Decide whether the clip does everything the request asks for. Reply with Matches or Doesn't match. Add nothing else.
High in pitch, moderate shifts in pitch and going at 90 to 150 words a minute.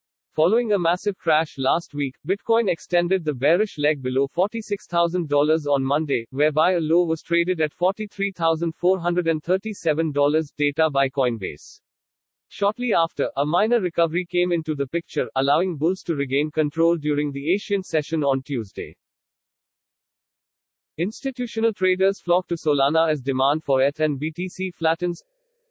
Doesn't match